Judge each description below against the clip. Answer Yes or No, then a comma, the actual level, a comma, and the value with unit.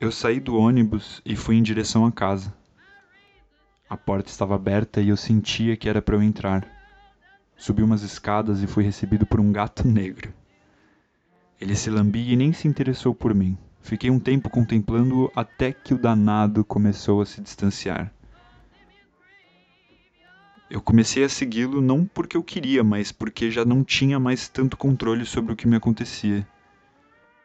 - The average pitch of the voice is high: No, low, 110 Hz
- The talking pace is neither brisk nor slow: Yes, average, 160 wpm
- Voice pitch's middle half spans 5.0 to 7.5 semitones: No, average, 3.7 semitones